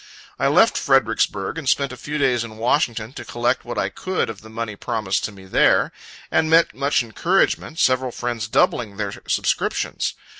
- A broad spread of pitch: No, average, 4.1 semitones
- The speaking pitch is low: Yes, low, 120 Hz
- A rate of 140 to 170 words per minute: No, average, 180 wpm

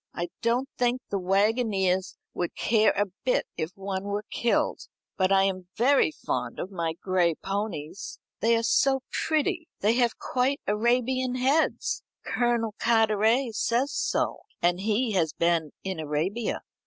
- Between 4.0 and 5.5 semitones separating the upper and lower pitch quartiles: Yes, average, 4.6 semitones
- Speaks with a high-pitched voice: Yes, high, 215 Hz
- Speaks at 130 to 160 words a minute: Yes, average, 145 wpm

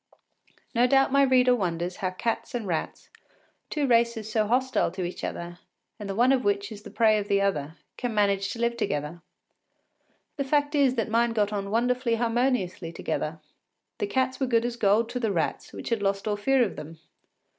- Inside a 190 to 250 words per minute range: Yes, average, 200 wpm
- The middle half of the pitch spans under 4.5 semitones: Yes, average, 4.0 semitones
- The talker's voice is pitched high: Yes, high, 225 Hz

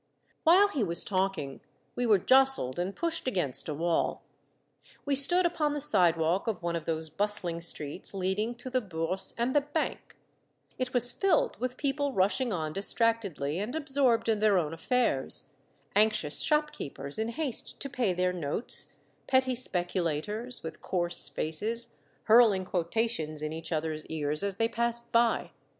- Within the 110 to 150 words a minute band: No, average, 160 wpm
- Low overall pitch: No, high, 210 Hz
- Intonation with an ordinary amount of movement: No, wide, 7.0 semitones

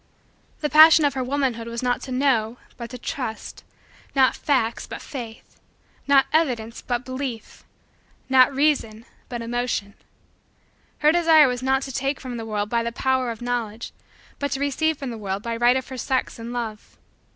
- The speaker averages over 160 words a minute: Yes, average, 175 wpm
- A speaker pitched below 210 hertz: No, very high, 250 Hz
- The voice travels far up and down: No, average, 2.9 semitones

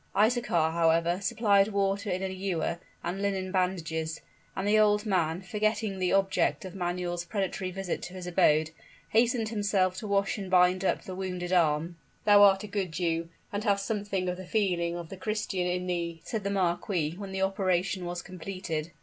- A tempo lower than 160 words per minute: No, average, 185 wpm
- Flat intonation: Yes, narrow, 2.3 semitones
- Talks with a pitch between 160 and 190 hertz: Yes, medium, 185 Hz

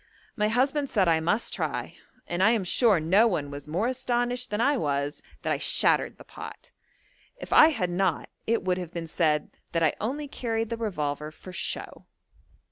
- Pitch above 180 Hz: Yes, high, 190 Hz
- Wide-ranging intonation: Yes, wide, 6.6 semitones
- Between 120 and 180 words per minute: No, average, 190 wpm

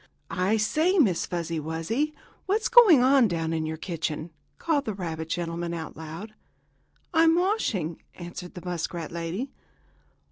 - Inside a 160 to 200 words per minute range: No, average, 140 wpm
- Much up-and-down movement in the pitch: Yes, wide, 8.8 semitones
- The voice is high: No, medium, 180 Hz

